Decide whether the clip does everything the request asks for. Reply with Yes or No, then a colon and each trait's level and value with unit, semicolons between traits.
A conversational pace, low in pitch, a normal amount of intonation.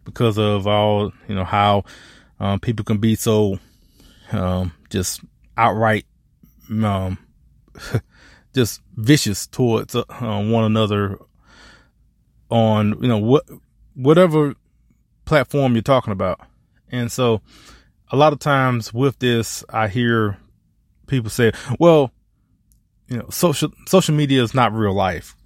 No: slow, 125 wpm; low, 110 Hz; average, 3.7 semitones